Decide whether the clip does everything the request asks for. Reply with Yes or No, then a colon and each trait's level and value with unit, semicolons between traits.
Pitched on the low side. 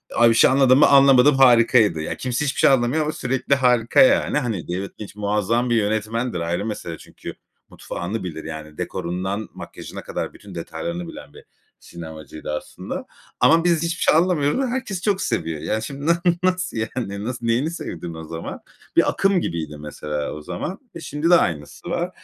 Yes: low, 115 Hz